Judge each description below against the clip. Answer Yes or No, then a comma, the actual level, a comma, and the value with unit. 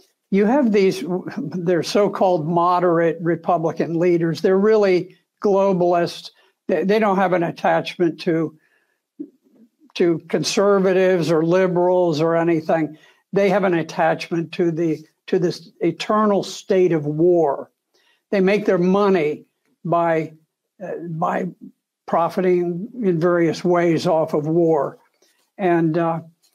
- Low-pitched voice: No, medium, 175 Hz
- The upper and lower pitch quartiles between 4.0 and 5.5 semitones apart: No, average, 2.8 semitones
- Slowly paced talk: Yes, slow, 115 wpm